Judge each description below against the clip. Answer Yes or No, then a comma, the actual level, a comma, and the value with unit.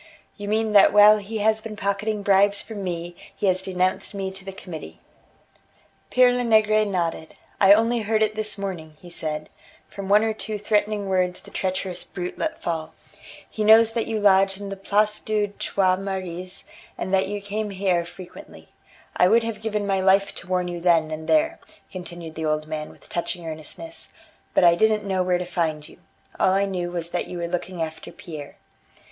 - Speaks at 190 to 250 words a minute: Yes, average, 195 wpm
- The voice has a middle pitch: No, high, 195 Hz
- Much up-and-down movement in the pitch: No, average, 3.2 semitones